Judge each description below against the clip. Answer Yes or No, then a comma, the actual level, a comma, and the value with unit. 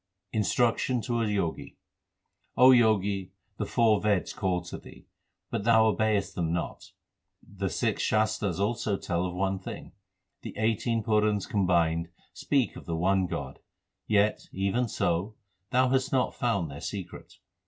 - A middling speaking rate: Yes, average, 145 wpm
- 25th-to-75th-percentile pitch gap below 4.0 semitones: Yes, average, 3.6 semitones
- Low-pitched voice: Yes, low, 100 Hz